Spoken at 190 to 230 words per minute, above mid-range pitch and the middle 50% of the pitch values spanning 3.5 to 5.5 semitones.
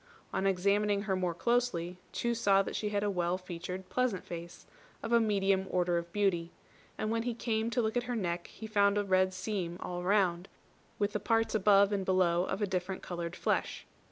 No: fast, 205 wpm; high, 195 Hz; average, 2.9 semitones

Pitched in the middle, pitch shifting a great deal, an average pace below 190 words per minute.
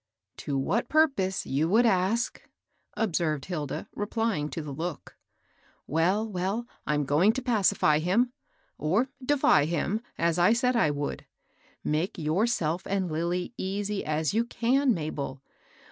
Yes: medium, 180 Hz; wide, 6.5 semitones; average, 145 wpm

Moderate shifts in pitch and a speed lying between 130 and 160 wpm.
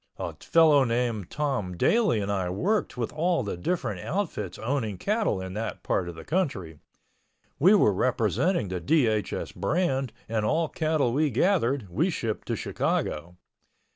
No: wide, 8.4 semitones; average, 155 wpm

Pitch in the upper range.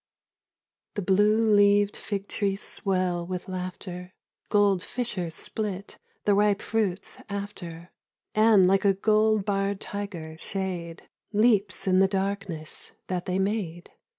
Yes: high, 195 Hz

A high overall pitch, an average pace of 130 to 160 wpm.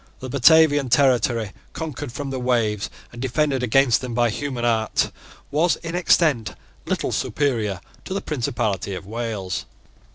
No: low, 125 Hz; average, 140 wpm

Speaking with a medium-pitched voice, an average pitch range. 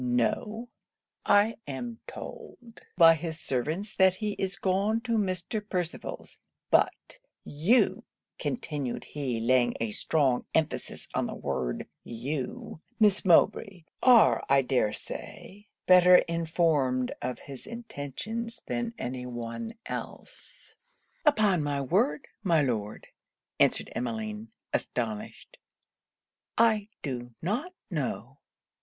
No: medium, 165 Hz; wide, 8.9 semitones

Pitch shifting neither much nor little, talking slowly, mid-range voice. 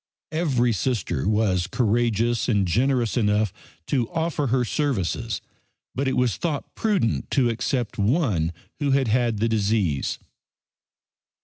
No: average, 4.2 semitones; slow, 125 wpm; low, 120 Hz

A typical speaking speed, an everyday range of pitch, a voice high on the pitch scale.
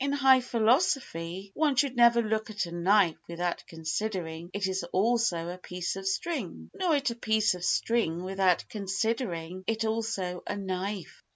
Yes: average, 170 wpm; average, 4.7 semitones; high, 200 Hz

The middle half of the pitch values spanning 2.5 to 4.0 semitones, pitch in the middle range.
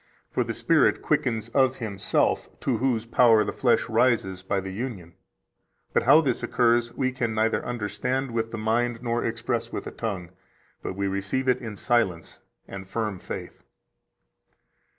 No: average, 3.3 semitones; low, 115 Hz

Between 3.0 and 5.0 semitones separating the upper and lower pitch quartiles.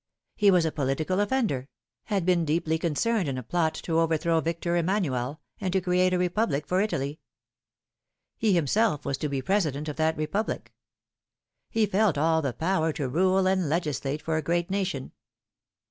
Yes: average, 4.0 semitones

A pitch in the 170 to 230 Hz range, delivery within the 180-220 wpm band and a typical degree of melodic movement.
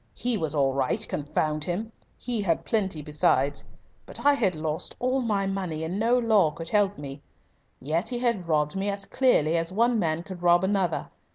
No: medium, 185 Hz; average, 190 wpm; wide, 5.8 semitones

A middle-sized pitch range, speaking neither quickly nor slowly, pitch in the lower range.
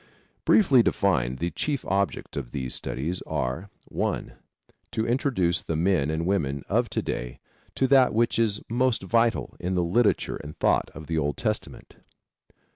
No: wide, 7.4 semitones; average, 160 wpm; very low, 90 Hz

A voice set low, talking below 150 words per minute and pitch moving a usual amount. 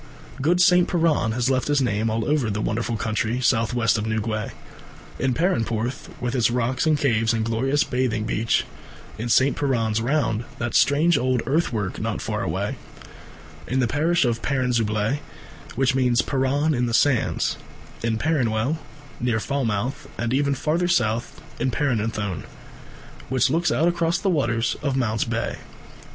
No: low, 125 Hz; average, 160 wpm; average, 3.9 semitones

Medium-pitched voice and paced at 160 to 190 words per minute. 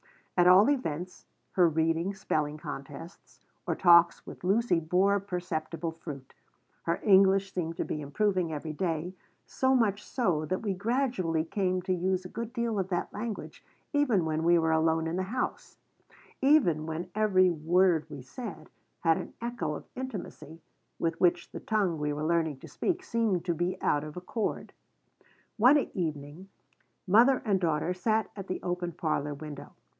Yes: medium, 180 Hz; average, 165 wpm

